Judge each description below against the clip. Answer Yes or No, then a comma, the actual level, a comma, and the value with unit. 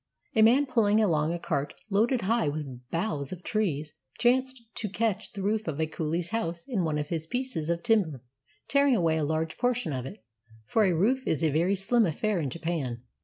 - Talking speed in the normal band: No, fast, 210 wpm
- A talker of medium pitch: Yes, medium, 175 Hz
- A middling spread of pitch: No, wide, 6.3 semitones